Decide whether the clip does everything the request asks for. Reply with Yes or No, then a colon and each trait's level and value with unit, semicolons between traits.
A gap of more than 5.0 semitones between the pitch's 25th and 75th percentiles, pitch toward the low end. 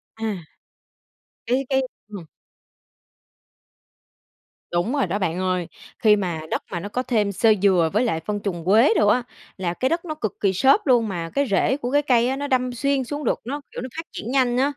No: wide, 5.5 semitones; high, 225 Hz